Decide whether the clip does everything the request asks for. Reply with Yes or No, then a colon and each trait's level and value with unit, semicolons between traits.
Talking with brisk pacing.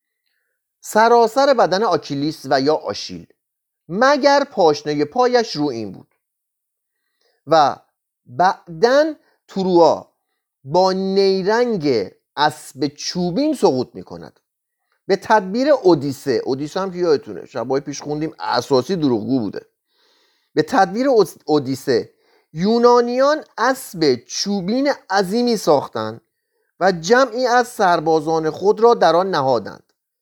No: slow, 105 wpm